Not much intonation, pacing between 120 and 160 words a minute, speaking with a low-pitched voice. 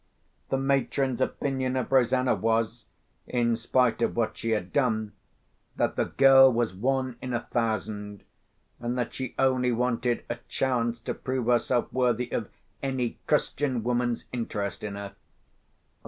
Yes: narrow, 2.2 semitones; average, 145 wpm; low, 120 Hz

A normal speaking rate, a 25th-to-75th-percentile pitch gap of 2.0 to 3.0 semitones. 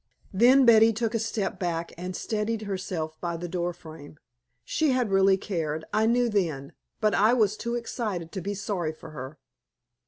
No: average, 180 wpm; average, 4.9 semitones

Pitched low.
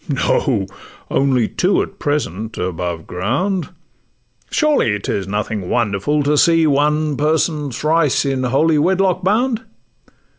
No: medium, 145 Hz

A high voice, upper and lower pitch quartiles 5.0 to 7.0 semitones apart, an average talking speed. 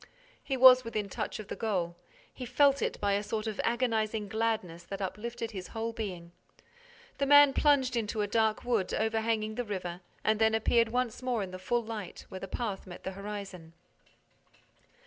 No: high, 220 Hz; average, 3.0 semitones; average, 185 wpm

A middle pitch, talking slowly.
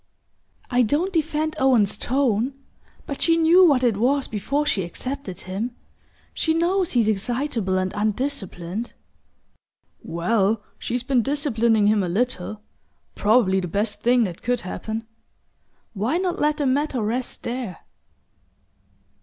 No: high, 240 Hz; slow, 130 wpm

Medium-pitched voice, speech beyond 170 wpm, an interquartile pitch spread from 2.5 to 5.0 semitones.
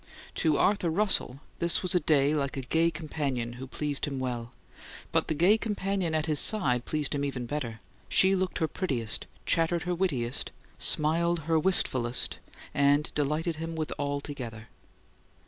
No: medium, 150 Hz; average, 165 wpm; average, 4.0 semitones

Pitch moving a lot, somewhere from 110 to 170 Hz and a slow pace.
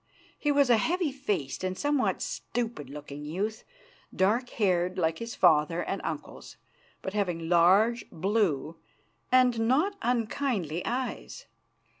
No: wide, 6.5 semitones; high, 210 Hz; slow, 125 wpm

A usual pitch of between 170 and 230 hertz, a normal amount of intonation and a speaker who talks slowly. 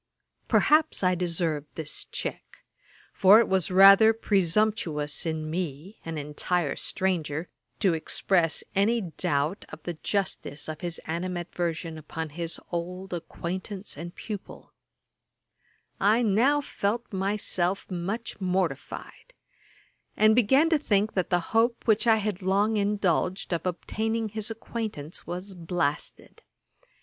Yes: medium, 185 Hz; average, 4.2 semitones; slow, 120 wpm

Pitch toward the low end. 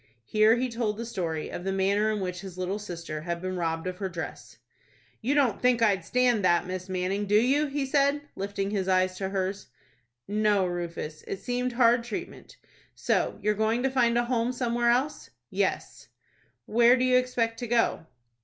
No: high, 210 Hz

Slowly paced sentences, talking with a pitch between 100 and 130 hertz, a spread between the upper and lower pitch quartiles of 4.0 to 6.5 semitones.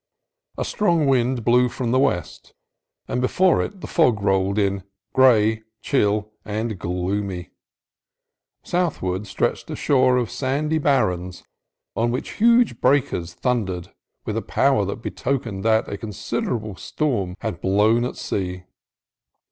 Yes: slow, 130 wpm; low, 115 Hz; average, 5.2 semitones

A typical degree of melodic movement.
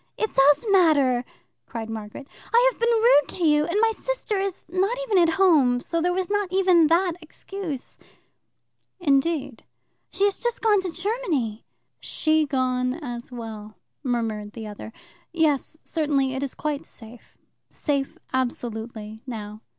No: wide, 7.3 semitones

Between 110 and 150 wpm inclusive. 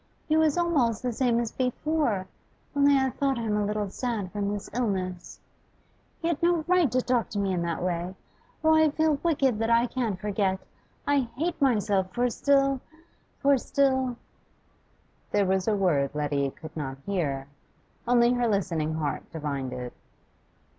No: average, 165 wpm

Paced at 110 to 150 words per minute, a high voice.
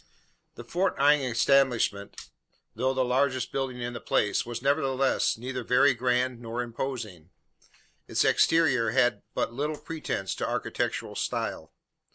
No: slow, 135 wpm; low, 125 Hz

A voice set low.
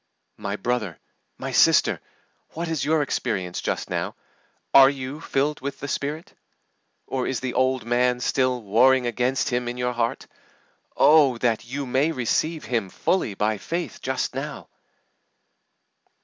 Yes: low, 130 Hz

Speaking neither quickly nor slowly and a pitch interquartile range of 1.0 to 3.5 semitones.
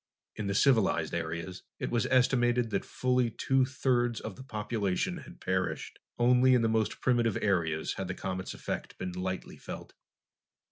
No: average, 160 wpm; average, 5.1 semitones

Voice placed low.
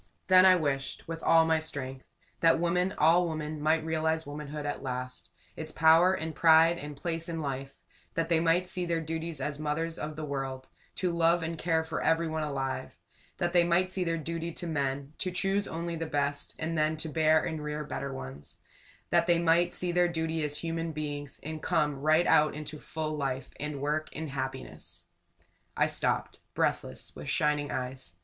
No: medium, 160 Hz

